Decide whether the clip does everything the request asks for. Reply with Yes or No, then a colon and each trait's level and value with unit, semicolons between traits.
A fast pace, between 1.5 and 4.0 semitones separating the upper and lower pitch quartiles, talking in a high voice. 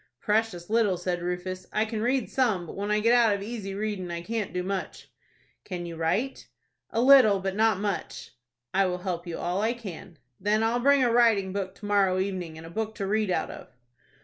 Yes: fast, 215 wpm; average, 3.5 semitones; high, 200 Hz